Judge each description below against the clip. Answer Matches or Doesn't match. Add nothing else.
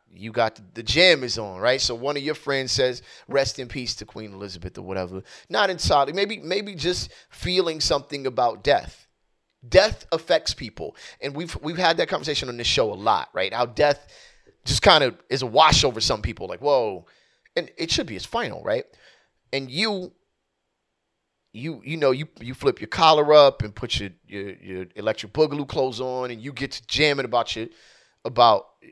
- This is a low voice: Matches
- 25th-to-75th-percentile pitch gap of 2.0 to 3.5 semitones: Doesn't match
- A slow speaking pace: Doesn't match